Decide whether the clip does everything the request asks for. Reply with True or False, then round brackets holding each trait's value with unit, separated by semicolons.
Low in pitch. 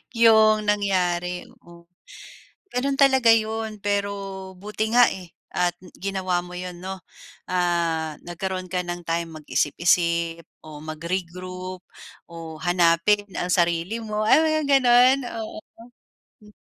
False (185 Hz)